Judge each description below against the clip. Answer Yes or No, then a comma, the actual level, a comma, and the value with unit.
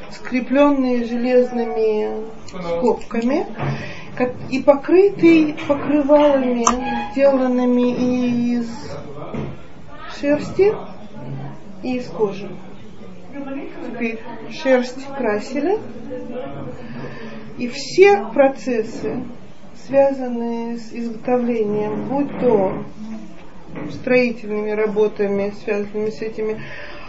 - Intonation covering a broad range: No, average, 3.8 semitones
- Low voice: No, high, 245 Hz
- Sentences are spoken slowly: Yes, slow, 65 wpm